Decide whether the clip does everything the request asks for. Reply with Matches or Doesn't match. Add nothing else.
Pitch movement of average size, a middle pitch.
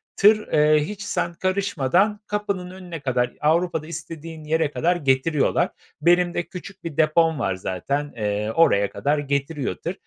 Matches